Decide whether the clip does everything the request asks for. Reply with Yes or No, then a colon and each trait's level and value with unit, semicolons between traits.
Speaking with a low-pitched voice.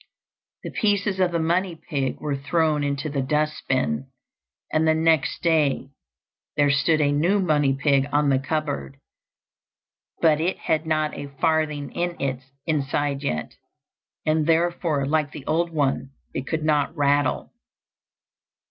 No: medium, 150 Hz